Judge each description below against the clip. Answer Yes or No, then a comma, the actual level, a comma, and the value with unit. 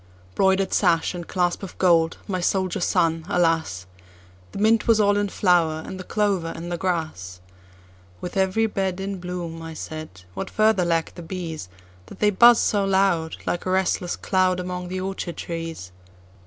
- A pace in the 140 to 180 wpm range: Yes, average, 145 wpm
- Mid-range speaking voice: Yes, medium, 175 Hz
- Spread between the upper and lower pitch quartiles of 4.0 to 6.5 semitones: No, average, 3.2 semitones